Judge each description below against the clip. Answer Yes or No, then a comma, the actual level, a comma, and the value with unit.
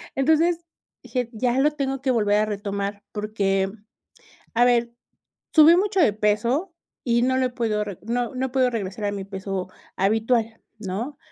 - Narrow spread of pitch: No, average, 4.2 semitones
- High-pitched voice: Yes, high, 235 Hz